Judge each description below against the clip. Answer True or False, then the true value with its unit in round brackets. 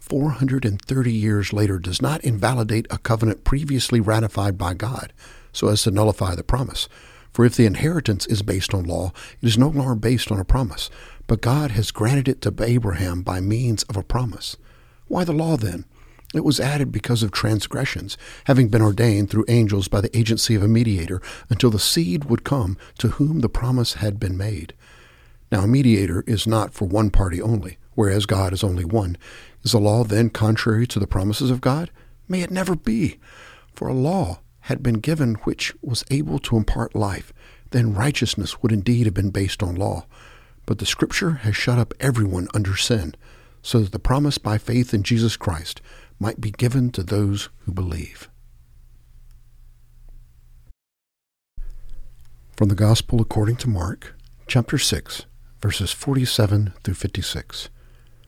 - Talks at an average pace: True (175 wpm)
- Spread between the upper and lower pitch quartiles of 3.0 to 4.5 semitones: True (3.9 semitones)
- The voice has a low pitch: True (110 Hz)